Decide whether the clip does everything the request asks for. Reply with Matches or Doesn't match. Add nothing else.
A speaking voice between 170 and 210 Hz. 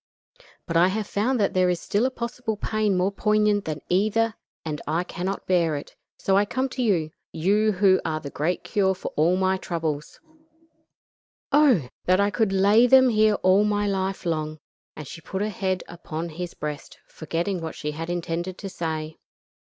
Matches